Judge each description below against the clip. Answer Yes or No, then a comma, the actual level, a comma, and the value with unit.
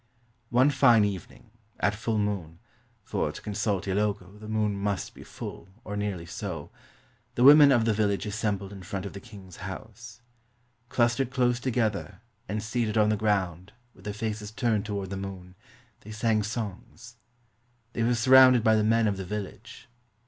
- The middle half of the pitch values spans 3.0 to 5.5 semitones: No, narrow, 2.6 semitones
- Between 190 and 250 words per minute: No, average, 170 wpm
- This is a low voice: Yes, low, 105 Hz